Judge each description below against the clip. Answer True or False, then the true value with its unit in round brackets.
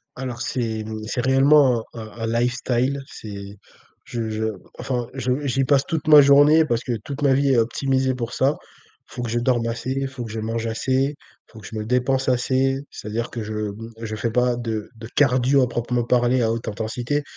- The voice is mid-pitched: False (125 Hz)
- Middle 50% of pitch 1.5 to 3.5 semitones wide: True (2.8 semitones)